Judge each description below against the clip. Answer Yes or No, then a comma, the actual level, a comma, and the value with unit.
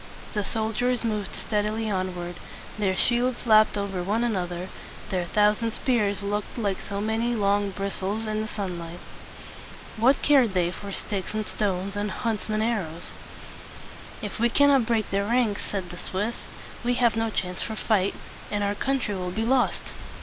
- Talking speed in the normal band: Yes, average, 175 wpm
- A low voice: No, high, 210 Hz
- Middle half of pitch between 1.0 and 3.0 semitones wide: Yes, average, 2.7 semitones